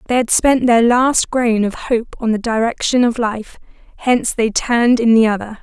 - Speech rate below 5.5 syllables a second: Yes, 4.8 syllables/s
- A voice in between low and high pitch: No, high, 230 Hz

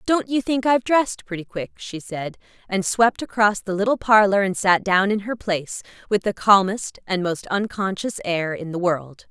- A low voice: No, high, 200 Hz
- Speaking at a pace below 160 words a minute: No, average, 200 wpm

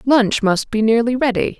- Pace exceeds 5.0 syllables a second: No, 4.7 syllables/s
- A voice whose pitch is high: Yes, high, 230 Hz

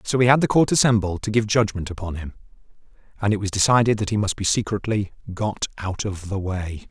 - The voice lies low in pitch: Yes, low, 105 Hz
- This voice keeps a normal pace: No, fast, 215 wpm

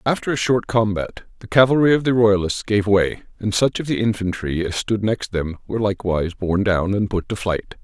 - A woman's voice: No, male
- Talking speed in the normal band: No, fast, 215 wpm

